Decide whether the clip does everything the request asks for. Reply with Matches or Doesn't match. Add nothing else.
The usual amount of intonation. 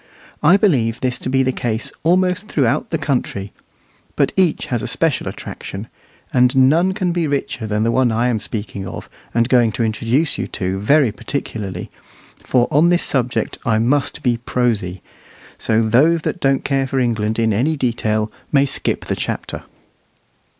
Matches